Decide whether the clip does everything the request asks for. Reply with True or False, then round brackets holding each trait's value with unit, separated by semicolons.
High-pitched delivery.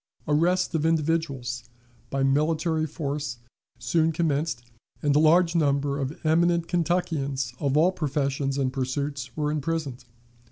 False (150 Hz)